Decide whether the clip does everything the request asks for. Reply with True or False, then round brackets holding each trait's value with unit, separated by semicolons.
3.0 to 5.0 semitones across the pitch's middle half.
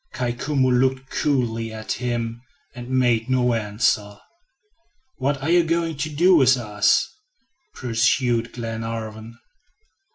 False (2.6 semitones)